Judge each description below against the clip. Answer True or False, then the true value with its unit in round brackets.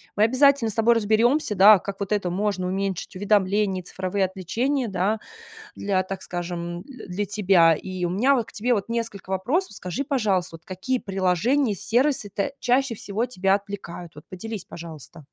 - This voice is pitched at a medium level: False (200 Hz)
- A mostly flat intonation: False (3.8 semitones)